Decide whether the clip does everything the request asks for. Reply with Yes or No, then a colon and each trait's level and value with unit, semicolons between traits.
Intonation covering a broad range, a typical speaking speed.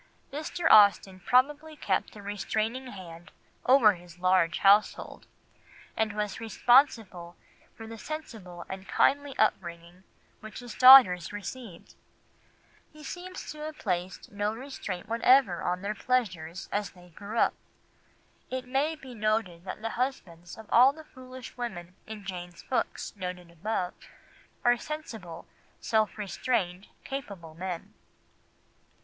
No: wide, 5.9 semitones; slow, 130 wpm